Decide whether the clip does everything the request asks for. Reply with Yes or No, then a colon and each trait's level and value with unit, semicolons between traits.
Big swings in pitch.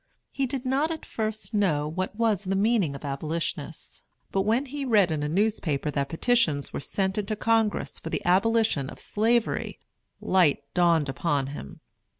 Yes: wide, 6.7 semitones